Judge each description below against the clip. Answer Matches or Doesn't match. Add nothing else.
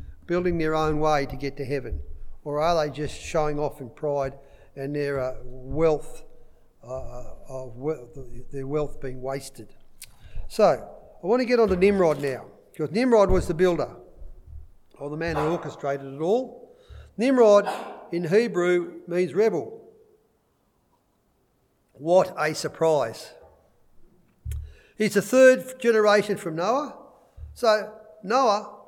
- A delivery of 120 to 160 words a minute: Matches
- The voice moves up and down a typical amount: Doesn't match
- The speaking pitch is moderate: Matches